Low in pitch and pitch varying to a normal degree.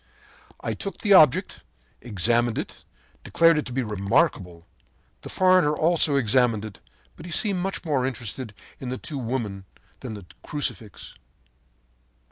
No: low, 130 Hz; wide, 6.5 semitones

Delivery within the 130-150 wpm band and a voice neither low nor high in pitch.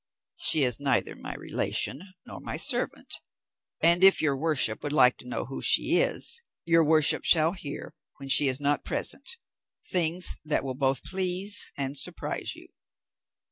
No: average, 160 wpm; medium, 150 Hz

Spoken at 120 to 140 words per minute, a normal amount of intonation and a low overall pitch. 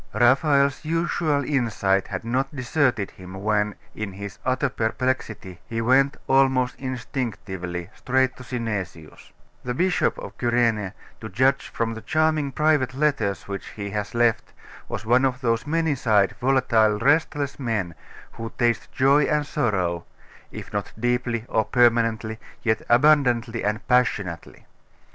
Yes: slow, 135 wpm; average, 4.0 semitones; low, 120 Hz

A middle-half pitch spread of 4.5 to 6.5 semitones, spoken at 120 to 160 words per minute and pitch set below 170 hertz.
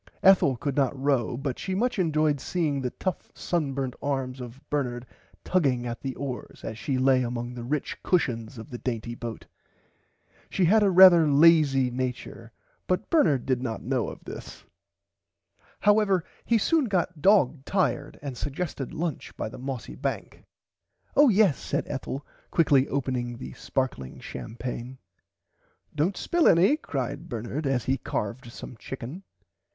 Yes: average, 5.3 semitones; average, 150 wpm; low, 135 Hz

